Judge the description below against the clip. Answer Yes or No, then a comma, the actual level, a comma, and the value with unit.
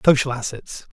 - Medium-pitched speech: No, low, 130 Hz